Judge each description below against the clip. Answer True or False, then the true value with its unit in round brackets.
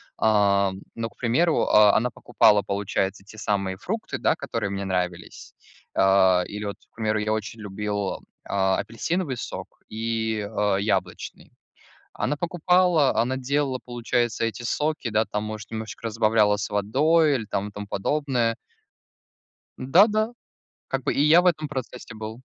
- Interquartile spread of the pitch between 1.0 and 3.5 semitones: False (4.6 semitones)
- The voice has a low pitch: True (110 Hz)